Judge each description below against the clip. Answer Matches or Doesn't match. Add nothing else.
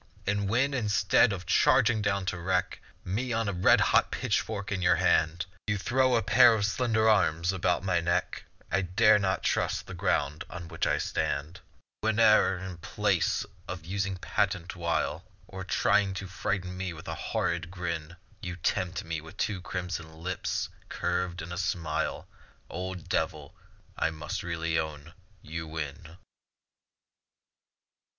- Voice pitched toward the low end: Matches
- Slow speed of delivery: Doesn't match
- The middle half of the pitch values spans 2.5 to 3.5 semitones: Matches